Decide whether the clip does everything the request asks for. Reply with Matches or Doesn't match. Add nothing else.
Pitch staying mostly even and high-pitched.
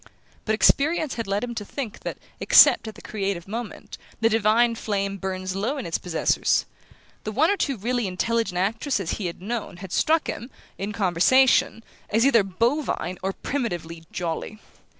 Doesn't match